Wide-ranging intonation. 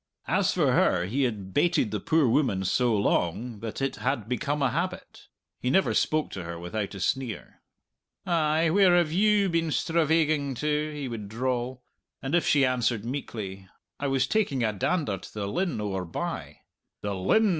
Yes: wide, 6.8 semitones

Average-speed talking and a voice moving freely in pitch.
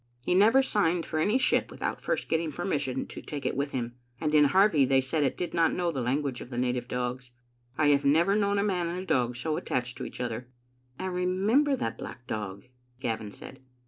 No: fast, 215 wpm; wide, 6.4 semitones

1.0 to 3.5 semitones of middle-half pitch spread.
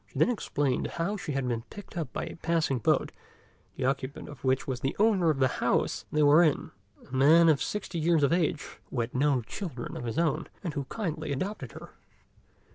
No: average, 4.2 semitones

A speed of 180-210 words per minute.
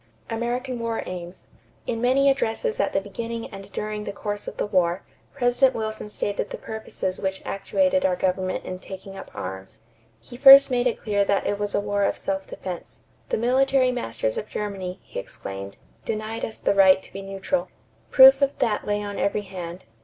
Yes: average, 190 wpm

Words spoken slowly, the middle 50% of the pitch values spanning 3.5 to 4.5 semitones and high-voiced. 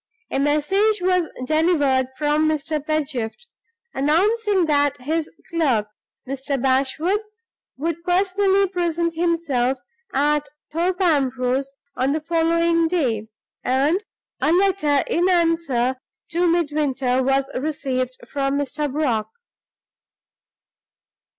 Yes: slow, 100 wpm; average, 4.0 semitones; very high, 300 Hz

